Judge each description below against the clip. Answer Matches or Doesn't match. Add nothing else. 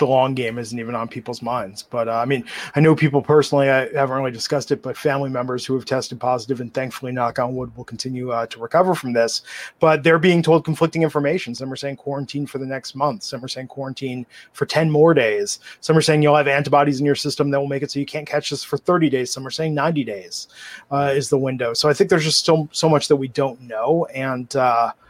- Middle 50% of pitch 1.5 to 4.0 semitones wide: Matches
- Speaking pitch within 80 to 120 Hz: Doesn't match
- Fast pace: Matches